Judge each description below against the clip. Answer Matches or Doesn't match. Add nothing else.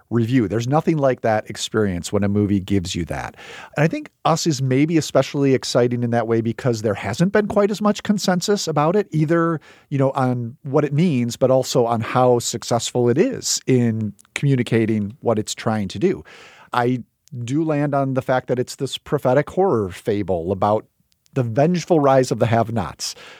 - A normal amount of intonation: Matches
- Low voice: Matches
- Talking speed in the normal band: Matches